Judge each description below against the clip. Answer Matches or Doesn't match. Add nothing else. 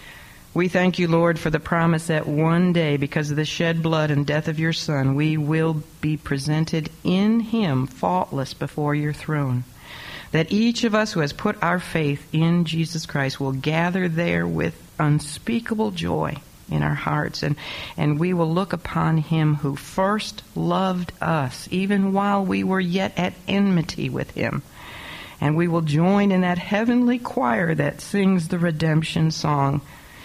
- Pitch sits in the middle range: Matches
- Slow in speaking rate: Doesn't match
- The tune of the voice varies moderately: Matches